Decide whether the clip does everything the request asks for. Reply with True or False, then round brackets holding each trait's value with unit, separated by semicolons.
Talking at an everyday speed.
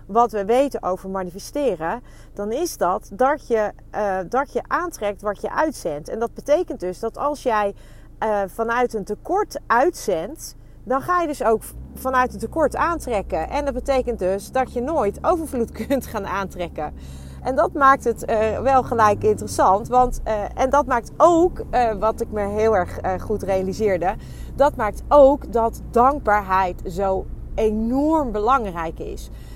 True (165 wpm)